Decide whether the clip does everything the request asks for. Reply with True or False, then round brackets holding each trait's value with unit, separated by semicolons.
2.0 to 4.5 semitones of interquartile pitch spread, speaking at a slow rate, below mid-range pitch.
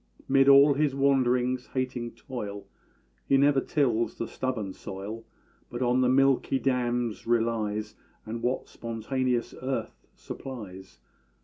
True (2.8 semitones; 120 wpm; 125 Hz)